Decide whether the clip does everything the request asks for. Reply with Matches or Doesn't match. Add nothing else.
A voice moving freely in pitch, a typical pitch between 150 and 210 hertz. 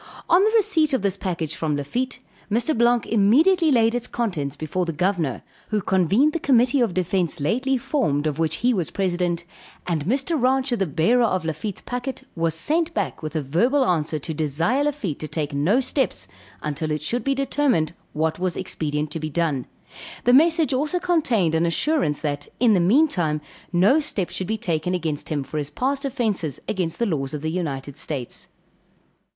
Matches